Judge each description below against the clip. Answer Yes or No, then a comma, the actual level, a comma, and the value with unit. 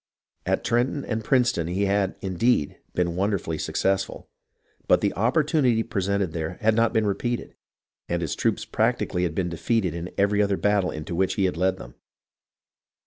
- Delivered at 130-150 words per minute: No, average, 165 wpm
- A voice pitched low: Yes, low, 100 Hz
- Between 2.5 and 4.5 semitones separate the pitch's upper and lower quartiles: Yes, average, 4.1 semitones